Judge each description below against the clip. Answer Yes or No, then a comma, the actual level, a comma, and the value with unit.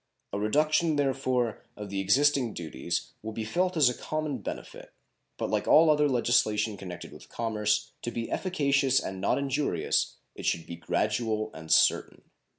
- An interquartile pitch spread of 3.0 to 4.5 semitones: No, wide, 5.4 semitones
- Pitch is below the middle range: Yes, low, 120 Hz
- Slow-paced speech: No, average, 160 wpm